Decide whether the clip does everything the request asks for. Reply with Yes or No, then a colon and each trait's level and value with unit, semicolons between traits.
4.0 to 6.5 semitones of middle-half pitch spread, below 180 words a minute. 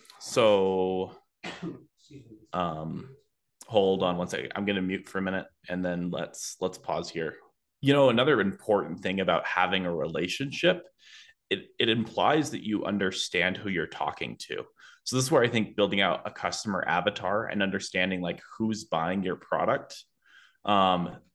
No: average, 3.6 semitones; average, 155 wpm